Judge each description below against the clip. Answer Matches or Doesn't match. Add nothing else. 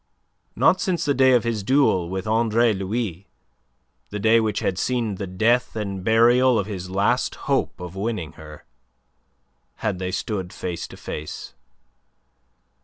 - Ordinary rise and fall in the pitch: Matches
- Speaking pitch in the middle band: Doesn't match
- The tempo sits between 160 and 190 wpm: Doesn't match